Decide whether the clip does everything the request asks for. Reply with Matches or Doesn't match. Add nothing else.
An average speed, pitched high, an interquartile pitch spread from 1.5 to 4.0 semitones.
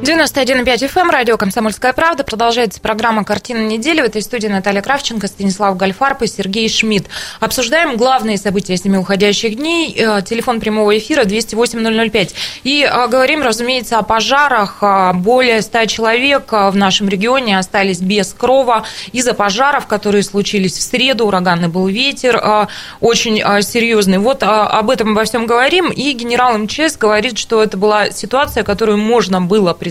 Matches